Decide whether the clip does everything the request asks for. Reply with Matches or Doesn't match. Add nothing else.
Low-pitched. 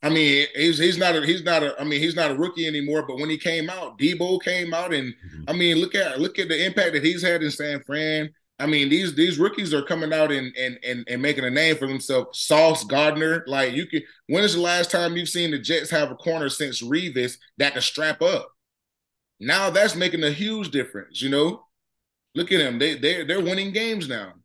Doesn't match